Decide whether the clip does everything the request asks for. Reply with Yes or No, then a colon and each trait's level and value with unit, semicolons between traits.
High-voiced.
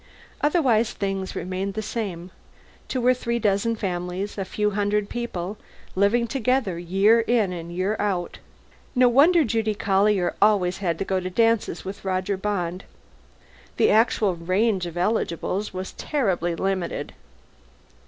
Yes: high, 200 Hz